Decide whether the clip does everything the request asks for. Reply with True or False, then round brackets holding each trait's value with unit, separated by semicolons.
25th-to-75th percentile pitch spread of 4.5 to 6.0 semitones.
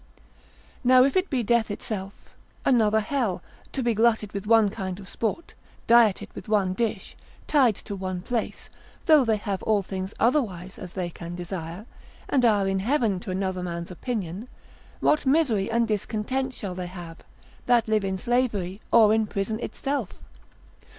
False (4.0 semitones)